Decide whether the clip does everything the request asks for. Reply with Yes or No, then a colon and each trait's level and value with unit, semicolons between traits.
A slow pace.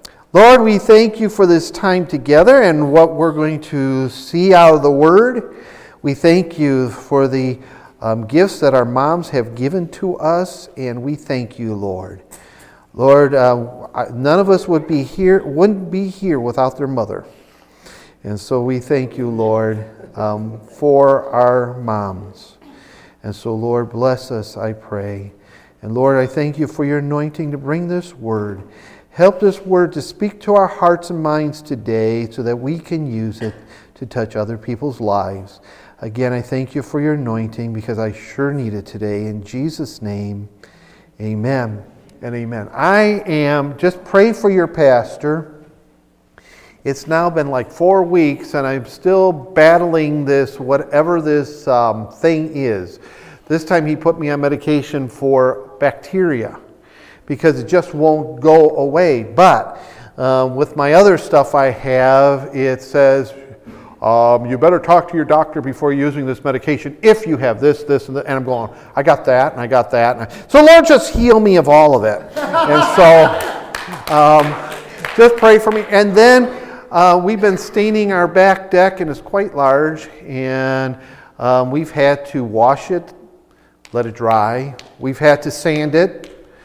No: average, 170 wpm